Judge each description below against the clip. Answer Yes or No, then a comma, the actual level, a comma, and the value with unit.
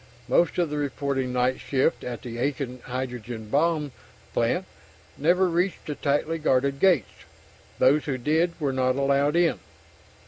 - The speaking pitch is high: No, medium, 140 Hz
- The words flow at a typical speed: Yes, average, 145 wpm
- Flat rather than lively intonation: No, average, 3.7 semitones